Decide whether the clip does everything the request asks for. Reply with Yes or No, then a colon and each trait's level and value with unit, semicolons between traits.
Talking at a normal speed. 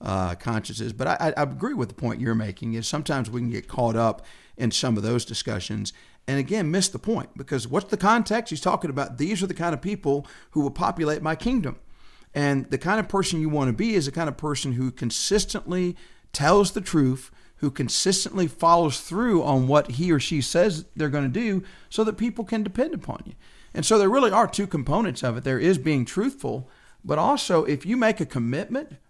No: fast, 220 wpm